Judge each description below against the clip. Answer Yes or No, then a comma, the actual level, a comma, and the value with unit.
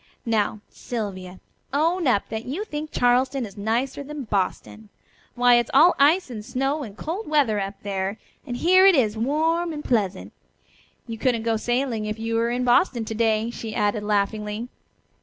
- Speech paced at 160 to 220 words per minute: Yes, average, 175 wpm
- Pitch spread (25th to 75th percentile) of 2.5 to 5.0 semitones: Yes, average, 4.6 semitones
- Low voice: No, high, 235 Hz